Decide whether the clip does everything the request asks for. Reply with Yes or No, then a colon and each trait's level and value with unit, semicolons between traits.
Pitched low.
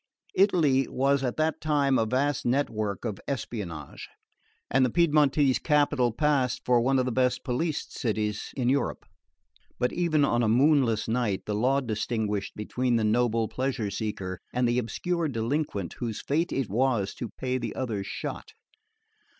Yes: low, 125 Hz